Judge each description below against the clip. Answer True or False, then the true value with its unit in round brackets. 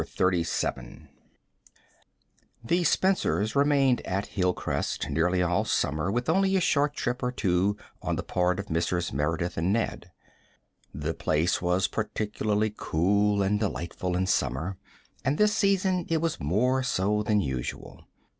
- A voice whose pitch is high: False (100 Hz)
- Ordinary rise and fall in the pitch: False (6.3 semitones)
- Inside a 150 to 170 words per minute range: False (140 wpm)